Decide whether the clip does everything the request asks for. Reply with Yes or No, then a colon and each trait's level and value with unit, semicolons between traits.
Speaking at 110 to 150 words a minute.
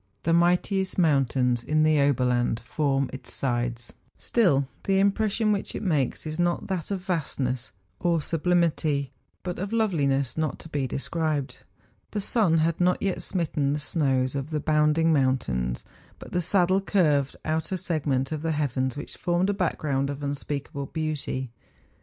No: average, 160 wpm